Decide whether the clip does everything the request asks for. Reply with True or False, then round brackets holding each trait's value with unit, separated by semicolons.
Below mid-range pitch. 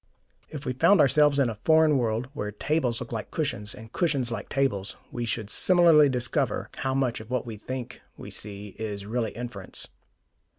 True (125 Hz)